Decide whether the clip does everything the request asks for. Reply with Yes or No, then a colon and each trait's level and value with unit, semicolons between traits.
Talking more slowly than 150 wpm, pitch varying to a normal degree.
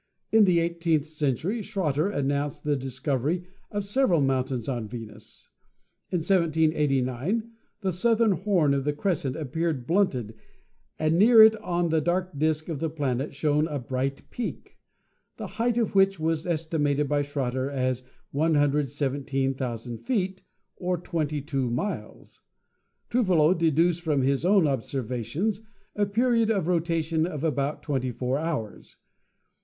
Yes: slow, 135 wpm; average, 4.8 semitones